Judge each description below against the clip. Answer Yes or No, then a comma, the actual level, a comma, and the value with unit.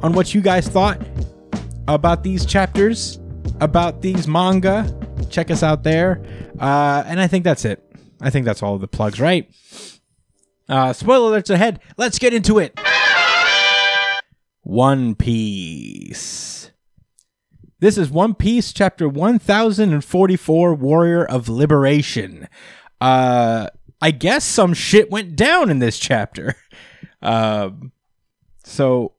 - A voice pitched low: No, medium, 160 Hz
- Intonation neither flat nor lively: No, wide, 7.3 semitones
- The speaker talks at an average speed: No, slow, 125 wpm